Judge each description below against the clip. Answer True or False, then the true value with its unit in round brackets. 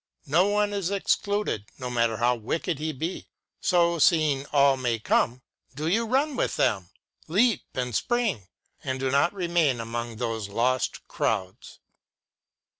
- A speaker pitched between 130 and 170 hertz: True (140 Hz)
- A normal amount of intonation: False (7.3 semitones)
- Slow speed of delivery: False (145 wpm)